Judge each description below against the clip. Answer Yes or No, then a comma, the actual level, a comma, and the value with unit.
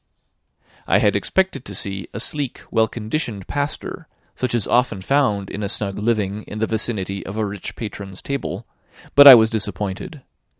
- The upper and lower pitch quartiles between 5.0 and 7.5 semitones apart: No, average, 3.9 semitones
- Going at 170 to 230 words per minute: Yes, average, 175 wpm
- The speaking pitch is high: No, low, 110 Hz